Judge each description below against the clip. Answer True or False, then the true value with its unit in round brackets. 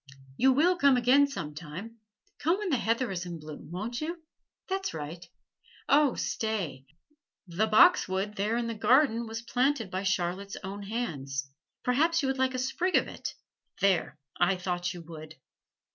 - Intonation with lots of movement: True (6.8 semitones)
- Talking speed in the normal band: True (165 wpm)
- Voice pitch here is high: True (220 Hz)